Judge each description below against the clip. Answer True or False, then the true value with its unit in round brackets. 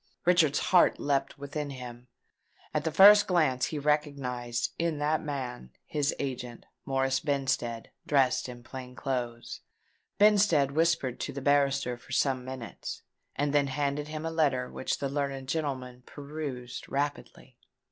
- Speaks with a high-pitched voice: False (140 Hz)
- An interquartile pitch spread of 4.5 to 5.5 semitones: False (2.7 semitones)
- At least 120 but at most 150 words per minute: True (140 wpm)